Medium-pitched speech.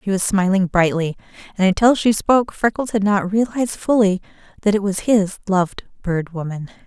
No: high, 200 Hz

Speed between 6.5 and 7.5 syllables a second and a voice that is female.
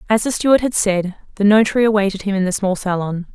Yes: 6.6 syllables/s; female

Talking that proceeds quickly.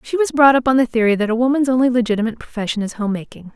Yes: fast, 255 wpm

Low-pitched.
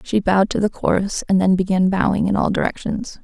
No: high, 195 Hz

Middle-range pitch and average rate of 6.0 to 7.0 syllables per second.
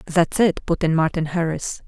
No: medium, 170 Hz; 4.7 syllables/s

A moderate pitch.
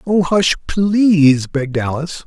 Yes: medium, 165 Hz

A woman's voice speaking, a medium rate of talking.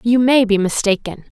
Yes: female; average, 170 wpm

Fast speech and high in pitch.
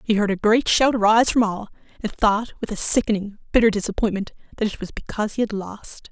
Yes: fast, 215 wpm; high, 210 Hz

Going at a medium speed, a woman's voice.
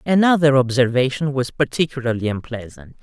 No: slow, 100 wpm; female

